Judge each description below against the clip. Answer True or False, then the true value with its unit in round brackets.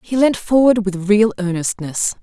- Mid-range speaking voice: False (205 Hz)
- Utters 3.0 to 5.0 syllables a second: True (4.4 syllables/s)